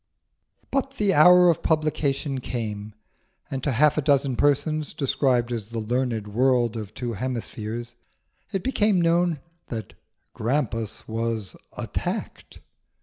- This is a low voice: Yes, low, 130 Hz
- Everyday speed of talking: No, slow, 125 wpm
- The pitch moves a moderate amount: Yes, average, 5.0 semitones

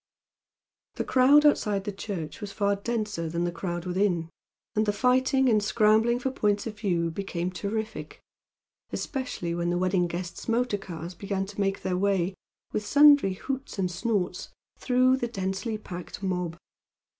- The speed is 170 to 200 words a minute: No, average, 155 wpm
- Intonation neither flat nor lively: Yes, average, 4.3 semitones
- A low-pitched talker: No, high, 200 Hz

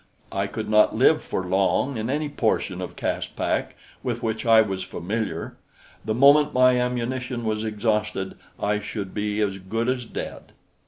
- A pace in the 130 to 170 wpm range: Yes, average, 160 wpm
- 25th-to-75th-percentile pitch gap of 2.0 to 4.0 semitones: Yes, average, 3.4 semitones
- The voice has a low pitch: Yes, low, 110 Hz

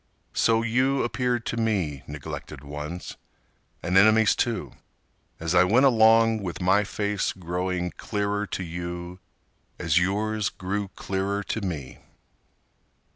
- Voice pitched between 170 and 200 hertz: No, low, 100 Hz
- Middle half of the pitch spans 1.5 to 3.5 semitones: No, average, 4.0 semitones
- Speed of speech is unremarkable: No, slow, 125 wpm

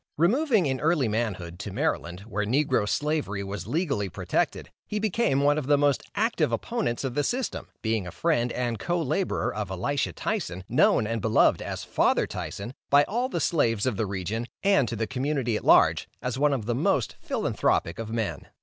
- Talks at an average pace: Yes, average, 190 wpm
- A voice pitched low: Yes, low, 125 Hz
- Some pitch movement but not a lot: No, wide, 6.3 semitones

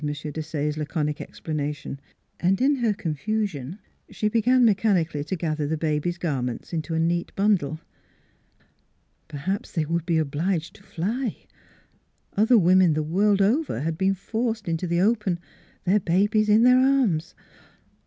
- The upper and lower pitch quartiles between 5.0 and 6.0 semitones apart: Yes, average, 5.3 semitones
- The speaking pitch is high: No, medium, 175 Hz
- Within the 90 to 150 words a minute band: Yes, average, 145 wpm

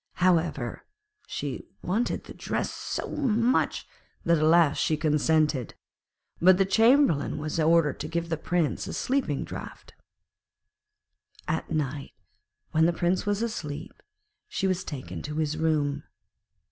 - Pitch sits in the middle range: Yes, medium, 160 Hz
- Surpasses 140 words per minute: No, slow, 135 wpm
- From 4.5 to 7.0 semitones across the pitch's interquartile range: No, average, 3.7 semitones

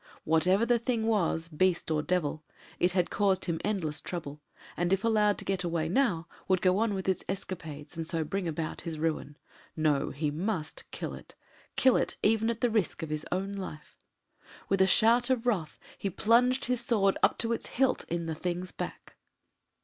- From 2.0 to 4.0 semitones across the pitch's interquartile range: No, average, 5.1 semitones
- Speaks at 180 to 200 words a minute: Yes, average, 195 wpm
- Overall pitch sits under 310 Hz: Yes, medium, 185 Hz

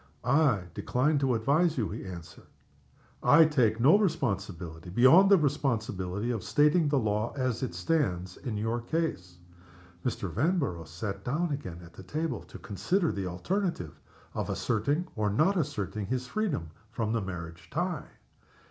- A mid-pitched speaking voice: No, low, 120 Hz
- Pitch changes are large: Yes, wide, 8.0 semitones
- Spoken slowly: No, average, 150 wpm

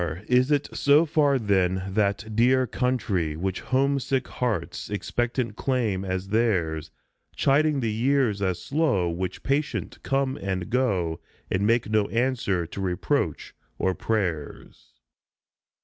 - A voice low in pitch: Yes, low, 110 Hz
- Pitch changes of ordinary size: No, wide, 5.7 semitones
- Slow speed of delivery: Yes, slow, 125 wpm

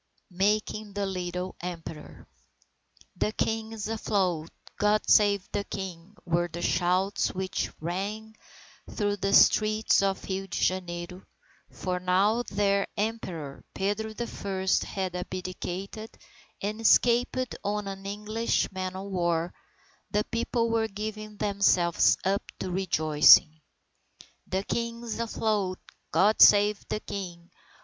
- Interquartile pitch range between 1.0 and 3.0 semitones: Yes, average, 2.7 semitones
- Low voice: No, high, 195 Hz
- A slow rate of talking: Yes, slow, 125 wpm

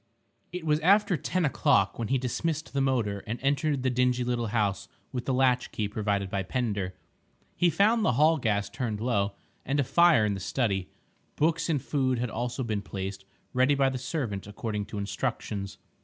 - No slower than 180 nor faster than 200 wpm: Yes, average, 185 wpm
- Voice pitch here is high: No, low, 125 Hz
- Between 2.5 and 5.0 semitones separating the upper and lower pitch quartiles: No, wide, 5.5 semitones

